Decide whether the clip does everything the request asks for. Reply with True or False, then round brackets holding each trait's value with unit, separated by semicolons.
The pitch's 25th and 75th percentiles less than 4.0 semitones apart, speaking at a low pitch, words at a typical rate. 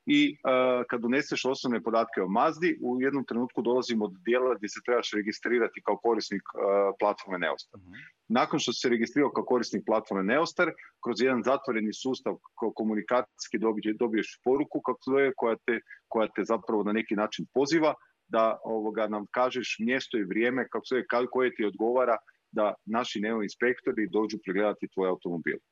False (2.9 semitones; 115 Hz; 165 wpm)